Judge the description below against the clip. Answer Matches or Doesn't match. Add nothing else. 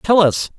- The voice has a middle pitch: Matches